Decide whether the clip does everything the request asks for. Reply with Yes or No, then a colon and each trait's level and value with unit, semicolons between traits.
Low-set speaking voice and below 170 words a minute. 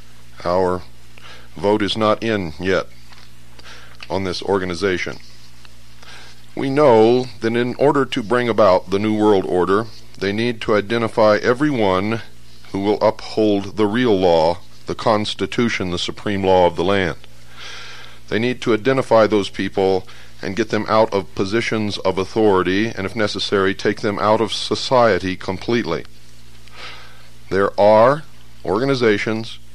Yes: low, 100 Hz; slow, 135 wpm